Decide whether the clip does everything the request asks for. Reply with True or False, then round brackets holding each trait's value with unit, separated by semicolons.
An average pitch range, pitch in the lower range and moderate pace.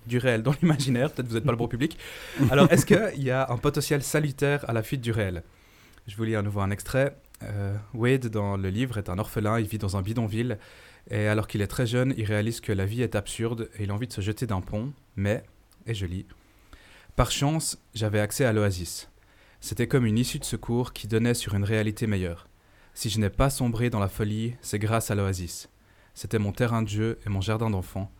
False (3.3 semitones; 110 Hz; 235 wpm)